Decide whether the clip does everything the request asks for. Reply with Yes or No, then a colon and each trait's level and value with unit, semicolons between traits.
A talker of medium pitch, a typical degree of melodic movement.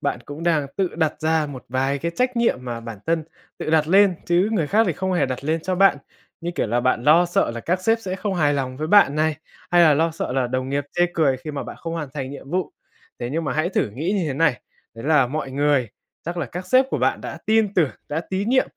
Yes: medium, 155 Hz; average, 4.5 semitones